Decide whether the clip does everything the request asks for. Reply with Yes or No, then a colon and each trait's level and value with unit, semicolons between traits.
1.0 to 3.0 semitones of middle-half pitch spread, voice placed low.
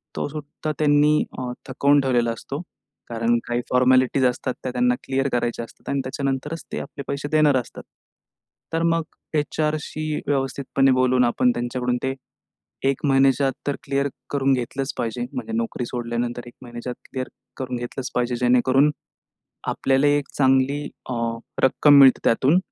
Yes: average, 2.7 semitones; low, 130 Hz